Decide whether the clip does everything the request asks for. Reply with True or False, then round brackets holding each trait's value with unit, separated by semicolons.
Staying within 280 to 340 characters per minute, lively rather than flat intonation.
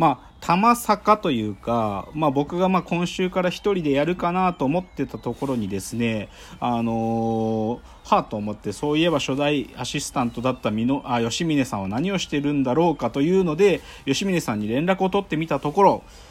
False (370 characters per minute; 7.2 semitones)